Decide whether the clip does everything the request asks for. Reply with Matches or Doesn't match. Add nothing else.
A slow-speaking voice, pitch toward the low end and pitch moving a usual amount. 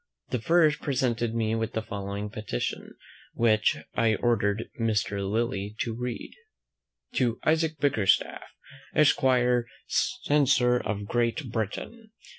Matches